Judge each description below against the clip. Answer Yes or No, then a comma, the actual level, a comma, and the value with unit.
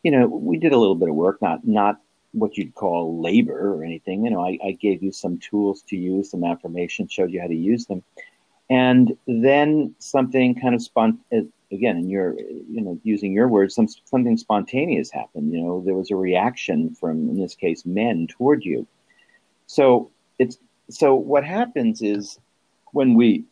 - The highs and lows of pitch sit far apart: Yes, wide, 6.3 semitones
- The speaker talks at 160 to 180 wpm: No, average, 190 wpm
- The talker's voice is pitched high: No, low, 105 Hz